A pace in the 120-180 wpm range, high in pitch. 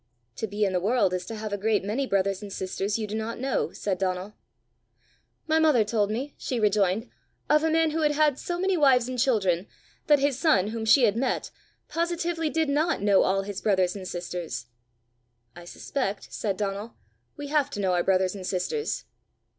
No: average, 200 wpm; high, 215 Hz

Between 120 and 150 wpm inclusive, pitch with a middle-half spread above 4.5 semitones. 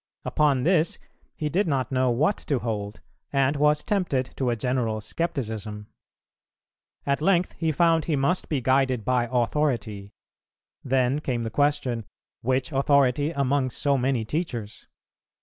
No: average, 140 wpm; average, 3.8 semitones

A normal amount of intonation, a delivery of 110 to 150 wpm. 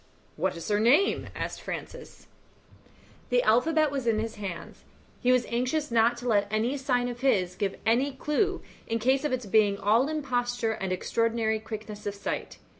No: average, 3.5 semitones; average, 175 wpm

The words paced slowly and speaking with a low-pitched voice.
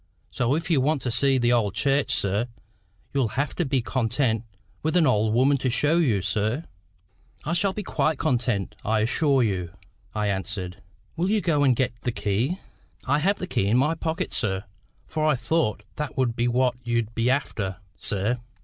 No: average, 190 wpm; low, 125 Hz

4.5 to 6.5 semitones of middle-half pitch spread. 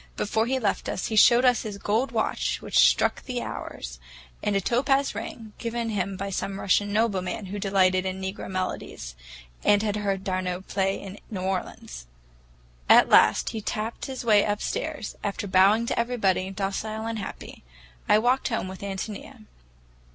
No: average, 2.9 semitones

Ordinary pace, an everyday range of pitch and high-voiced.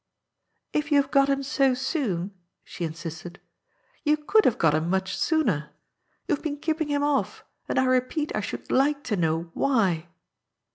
No: average, 180 wpm; wide, 8.8 semitones; very high, 260 Hz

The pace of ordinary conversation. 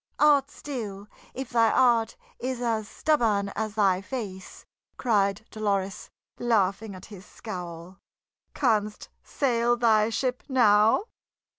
No: slow, 115 wpm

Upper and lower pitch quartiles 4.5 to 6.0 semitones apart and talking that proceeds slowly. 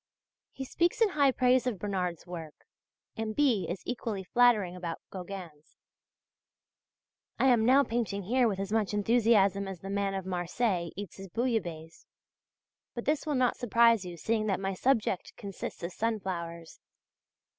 No: average, 4.8 semitones; average, 155 wpm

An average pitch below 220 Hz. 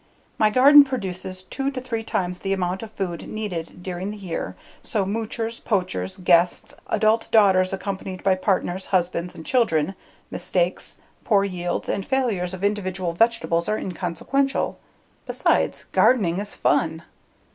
Yes: high, 190 Hz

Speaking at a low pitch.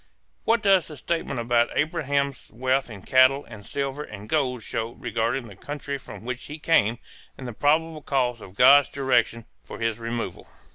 Yes: low, 130 Hz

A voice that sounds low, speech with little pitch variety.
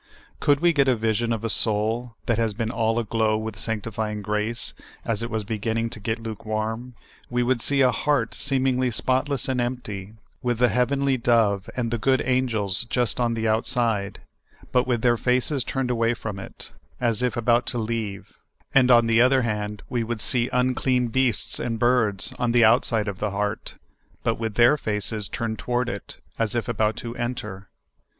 Yes: low, 115 Hz; narrow, 2.2 semitones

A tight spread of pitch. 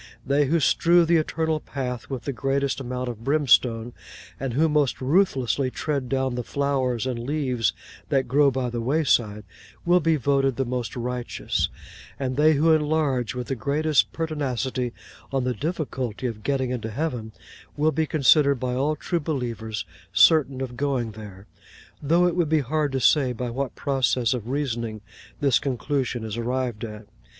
No: average, 3.4 semitones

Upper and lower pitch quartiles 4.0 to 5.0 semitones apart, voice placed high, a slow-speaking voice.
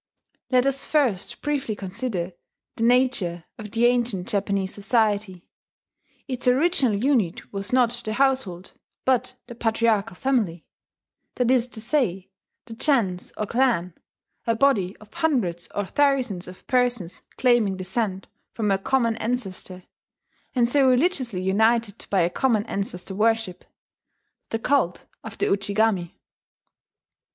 Yes: average, 4.6 semitones; high, 225 Hz; slow, 130 wpm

